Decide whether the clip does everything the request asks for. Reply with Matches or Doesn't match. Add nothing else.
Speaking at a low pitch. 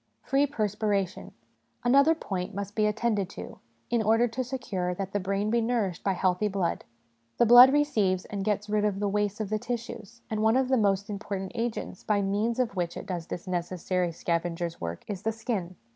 Doesn't match